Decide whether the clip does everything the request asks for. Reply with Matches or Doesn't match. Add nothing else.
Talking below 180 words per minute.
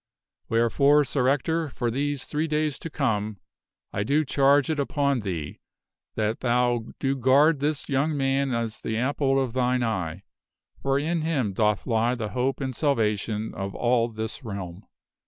Matches